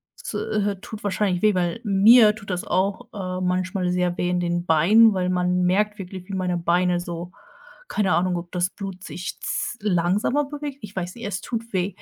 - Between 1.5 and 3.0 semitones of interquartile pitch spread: Yes, narrow, 2.6 semitones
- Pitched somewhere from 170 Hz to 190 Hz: Yes, medium, 185 Hz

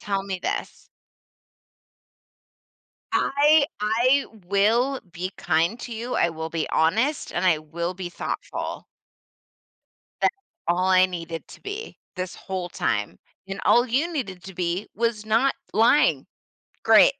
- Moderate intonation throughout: No, wide, 5.8 semitones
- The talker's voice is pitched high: Yes, high, 195 Hz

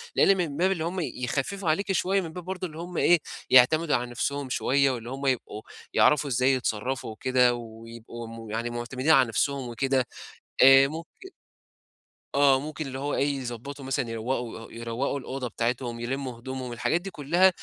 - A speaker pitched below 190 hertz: Yes, low, 135 Hz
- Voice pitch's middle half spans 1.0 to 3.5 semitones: No, average, 4.3 semitones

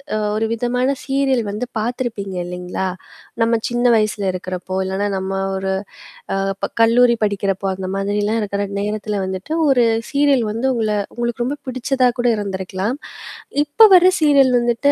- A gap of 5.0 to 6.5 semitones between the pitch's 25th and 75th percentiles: No, average, 4.2 semitones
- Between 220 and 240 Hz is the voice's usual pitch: Yes, high, 225 Hz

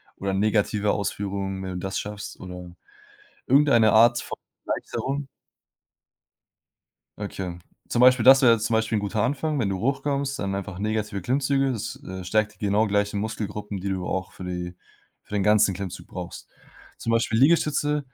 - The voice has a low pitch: Yes, low, 105 Hz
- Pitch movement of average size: Yes, average, 4.2 semitones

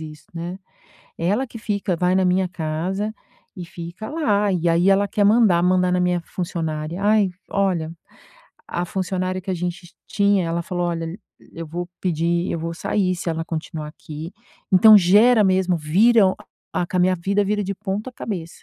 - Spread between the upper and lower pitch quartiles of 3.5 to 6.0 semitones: No, average, 2.9 semitones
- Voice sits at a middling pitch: Yes, medium, 180 Hz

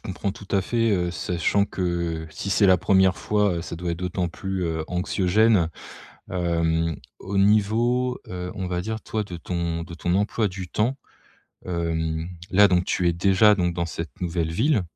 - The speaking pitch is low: Yes, very low, 90 Hz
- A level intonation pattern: No, average, 3.0 semitones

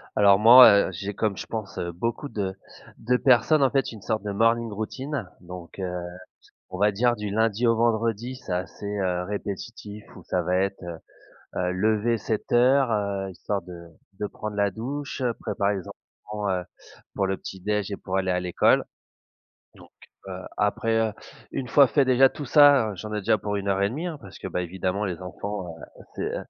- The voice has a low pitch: Yes, low, 105 Hz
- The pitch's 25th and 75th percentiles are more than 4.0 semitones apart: No, average, 3.6 semitones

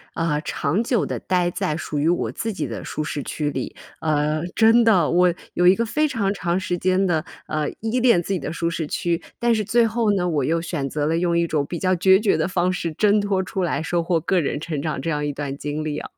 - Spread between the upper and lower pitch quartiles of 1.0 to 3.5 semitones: No, average, 4.0 semitones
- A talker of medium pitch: Yes, medium, 175 Hz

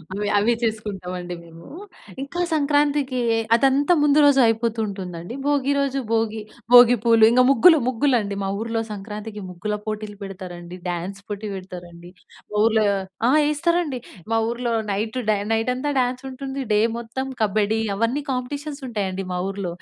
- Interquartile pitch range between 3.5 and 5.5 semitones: Yes, average, 5.0 semitones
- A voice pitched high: Yes, high, 225 Hz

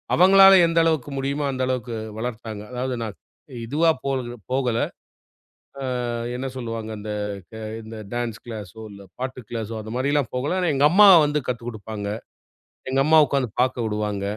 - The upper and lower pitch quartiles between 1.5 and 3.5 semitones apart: No, average, 4.0 semitones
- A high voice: No, low, 125 Hz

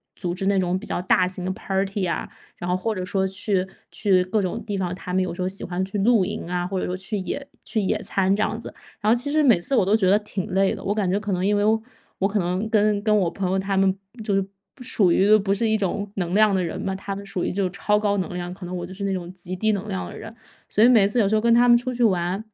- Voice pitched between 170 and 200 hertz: Yes, high, 195 Hz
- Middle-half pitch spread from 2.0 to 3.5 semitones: Yes, narrow, 2.4 semitones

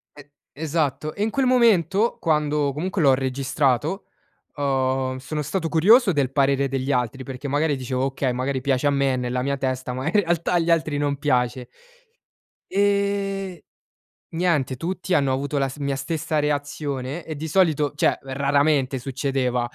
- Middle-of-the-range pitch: Yes, medium, 145 Hz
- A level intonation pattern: No, average, 3.6 semitones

